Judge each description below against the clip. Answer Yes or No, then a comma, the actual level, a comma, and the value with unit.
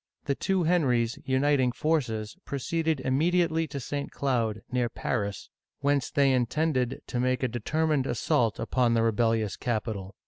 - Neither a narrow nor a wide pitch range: Yes, average, 3.9 semitones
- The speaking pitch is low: Yes, low, 130 Hz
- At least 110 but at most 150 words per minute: Yes, average, 140 wpm